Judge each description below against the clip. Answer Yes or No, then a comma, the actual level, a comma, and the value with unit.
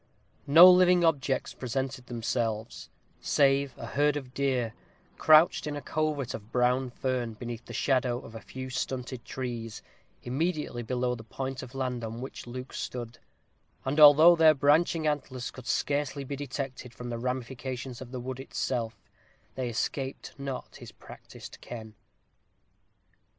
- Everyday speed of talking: Yes, average, 145 wpm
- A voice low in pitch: Yes, low, 130 Hz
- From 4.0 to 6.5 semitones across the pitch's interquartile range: No, average, 2.7 semitones